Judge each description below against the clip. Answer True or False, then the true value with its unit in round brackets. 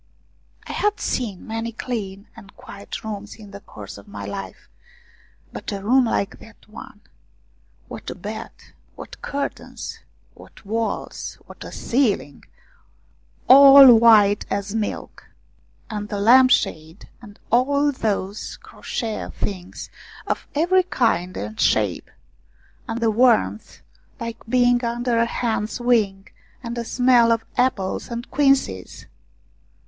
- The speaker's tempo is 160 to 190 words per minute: False (135 wpm)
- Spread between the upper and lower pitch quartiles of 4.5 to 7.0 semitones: False (3.6 semitones)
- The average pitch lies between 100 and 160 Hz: False (225 Hz)